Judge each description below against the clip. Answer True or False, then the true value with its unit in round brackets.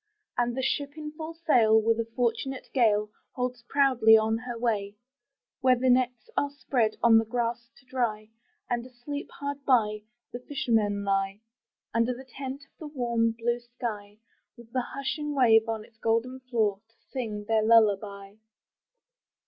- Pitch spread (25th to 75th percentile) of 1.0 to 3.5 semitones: True (2.8 semitones)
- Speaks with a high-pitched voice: True (235 Hz)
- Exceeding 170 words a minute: False (160 wpm)